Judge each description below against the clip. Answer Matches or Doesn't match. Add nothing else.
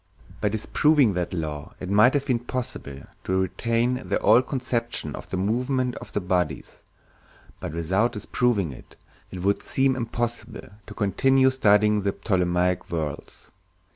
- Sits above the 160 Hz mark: Doesn't match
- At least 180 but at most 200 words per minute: Doesn't match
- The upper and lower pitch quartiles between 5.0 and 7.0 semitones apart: Matches